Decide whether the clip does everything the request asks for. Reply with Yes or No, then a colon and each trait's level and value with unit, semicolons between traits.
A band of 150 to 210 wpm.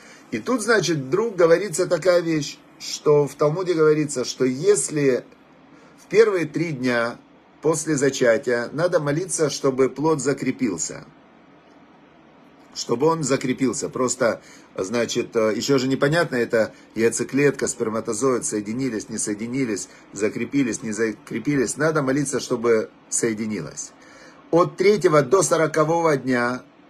No: slow, 110 wpm